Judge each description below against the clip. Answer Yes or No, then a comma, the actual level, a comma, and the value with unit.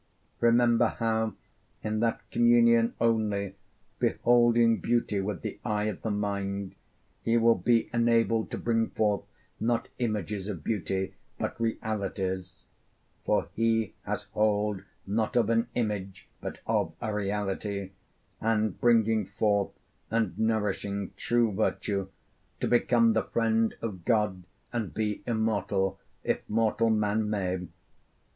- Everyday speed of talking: No, slow, 125 wpm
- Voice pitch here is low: Yes, low, 110 Hz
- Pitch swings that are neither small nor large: No, narrow, 2.3 semitones